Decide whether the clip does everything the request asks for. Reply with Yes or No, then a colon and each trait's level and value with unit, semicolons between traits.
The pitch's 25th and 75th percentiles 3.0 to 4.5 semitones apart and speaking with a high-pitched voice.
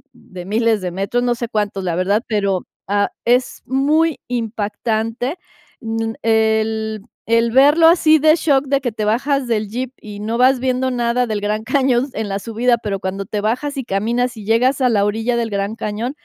Yes: average, 3.3 semitones; high, 230 Hz